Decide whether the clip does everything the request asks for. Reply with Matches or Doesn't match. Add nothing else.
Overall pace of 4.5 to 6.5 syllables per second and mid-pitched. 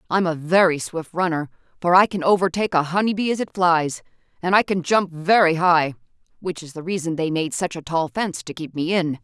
Matches